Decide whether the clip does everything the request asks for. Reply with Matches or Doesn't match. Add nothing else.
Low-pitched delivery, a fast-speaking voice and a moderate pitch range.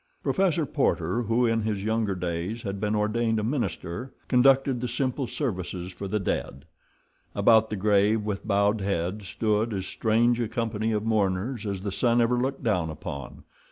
Doesn't match